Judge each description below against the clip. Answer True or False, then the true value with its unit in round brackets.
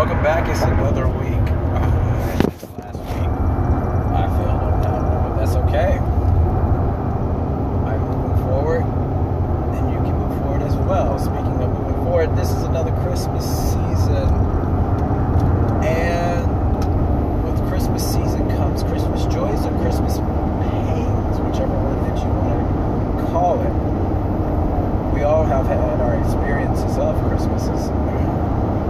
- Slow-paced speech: True (125 wpm)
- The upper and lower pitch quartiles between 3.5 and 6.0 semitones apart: False (2.7 semitones)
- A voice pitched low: True (95 Hz)